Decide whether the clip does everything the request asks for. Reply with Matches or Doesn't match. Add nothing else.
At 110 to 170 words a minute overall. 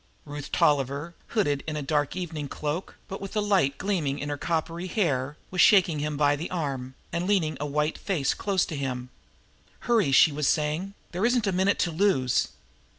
Doesn't match